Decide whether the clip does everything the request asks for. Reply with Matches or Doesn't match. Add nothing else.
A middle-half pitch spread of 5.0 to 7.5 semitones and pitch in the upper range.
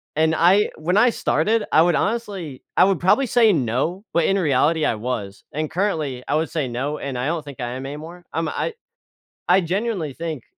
Doesn't match